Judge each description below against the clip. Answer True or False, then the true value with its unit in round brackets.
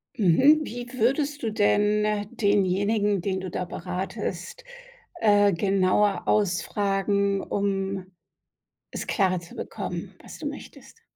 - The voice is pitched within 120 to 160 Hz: False (200 Hz)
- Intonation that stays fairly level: True (1.9 semitones)